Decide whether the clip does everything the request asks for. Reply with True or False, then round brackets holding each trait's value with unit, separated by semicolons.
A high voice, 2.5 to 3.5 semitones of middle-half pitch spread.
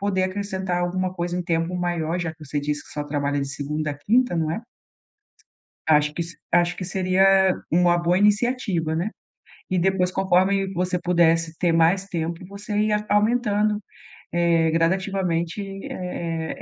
False (175 Hz; 2.8 semitones)